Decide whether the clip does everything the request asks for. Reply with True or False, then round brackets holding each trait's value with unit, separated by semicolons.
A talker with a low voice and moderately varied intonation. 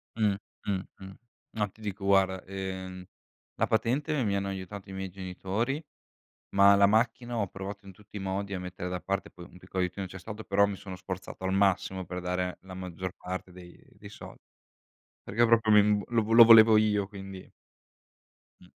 False (95 Hz; 2.1 semitones)